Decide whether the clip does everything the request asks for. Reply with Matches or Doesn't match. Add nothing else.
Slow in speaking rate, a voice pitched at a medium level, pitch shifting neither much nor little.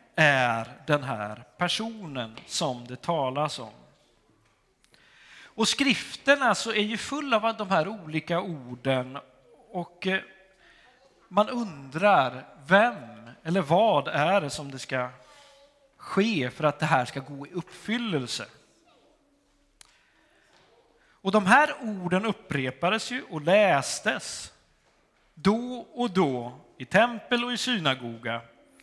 Doesn't match